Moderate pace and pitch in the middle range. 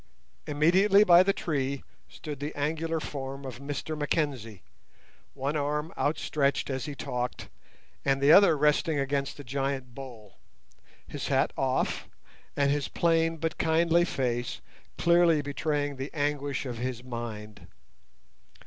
No: slow, 130 wpm; medium, 145 Hz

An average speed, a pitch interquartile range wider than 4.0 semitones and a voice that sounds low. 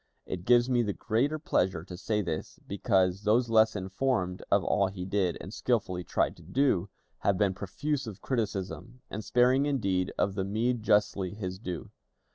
Yes: average, 175 wpm; average, 4.4 semitones; low, 100 Hz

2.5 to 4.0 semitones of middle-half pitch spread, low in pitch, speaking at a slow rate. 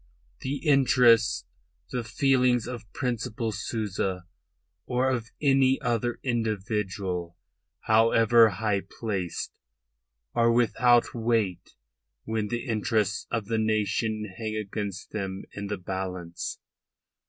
Yes: average, 3.2 semitones; low, 110 Hz; slow, 105 wpm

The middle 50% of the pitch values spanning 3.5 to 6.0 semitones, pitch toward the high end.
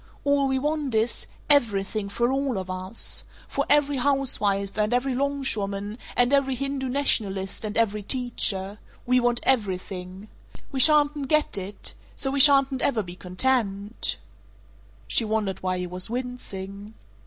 Yes: wide, 5.4 semitones; high, 235 Hz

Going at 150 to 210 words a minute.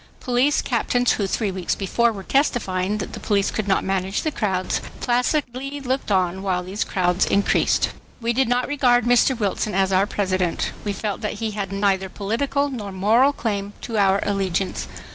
Yes: average, 180 wpm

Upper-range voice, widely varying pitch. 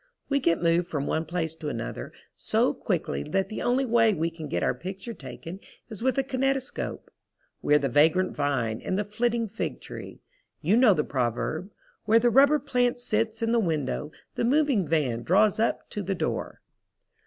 Yes: high, 195 Hz; wide, 7.2 semitones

